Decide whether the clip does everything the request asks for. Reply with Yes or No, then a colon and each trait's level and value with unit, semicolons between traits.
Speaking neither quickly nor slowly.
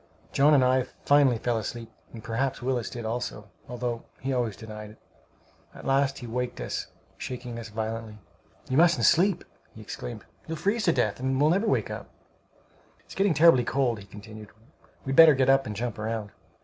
Yes: average, 180 wpm